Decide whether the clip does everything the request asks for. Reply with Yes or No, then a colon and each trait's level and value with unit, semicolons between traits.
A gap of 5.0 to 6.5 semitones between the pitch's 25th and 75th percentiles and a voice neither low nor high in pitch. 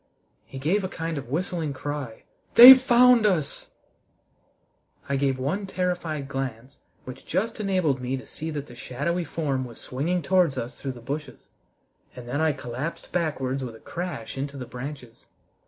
Yes: average, 5.3 semitones; medium, 145 Hz